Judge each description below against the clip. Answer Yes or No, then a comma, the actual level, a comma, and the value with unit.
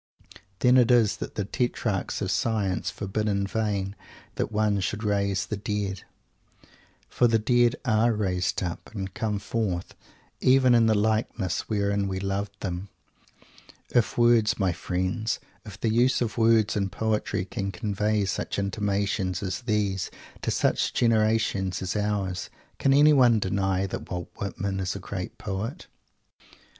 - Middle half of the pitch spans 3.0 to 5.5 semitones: No, narrow, 2.5 semitones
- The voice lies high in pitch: No, low, 105 Hz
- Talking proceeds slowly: No, average, 150 wpm